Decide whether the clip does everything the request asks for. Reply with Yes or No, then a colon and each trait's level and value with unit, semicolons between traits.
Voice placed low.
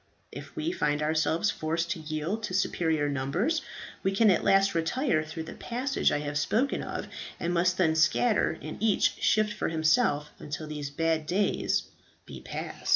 No: medium, 165 Hz